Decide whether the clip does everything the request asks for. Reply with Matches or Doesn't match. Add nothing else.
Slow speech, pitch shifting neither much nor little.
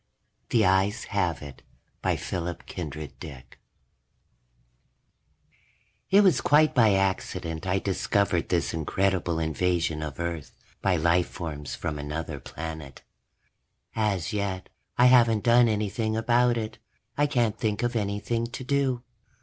Doesn't match